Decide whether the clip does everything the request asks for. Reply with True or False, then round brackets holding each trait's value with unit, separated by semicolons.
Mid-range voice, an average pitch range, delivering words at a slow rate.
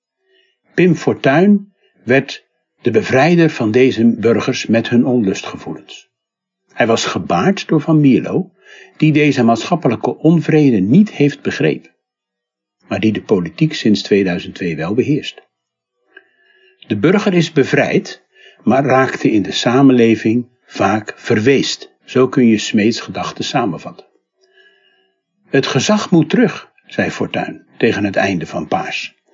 False (155 Hz; 8.3 semitones; 125 wpm)